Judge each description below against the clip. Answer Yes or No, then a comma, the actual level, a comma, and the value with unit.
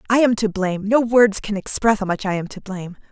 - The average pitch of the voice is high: Yes, high, 205 Hz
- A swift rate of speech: Yes, fast, 270 wpm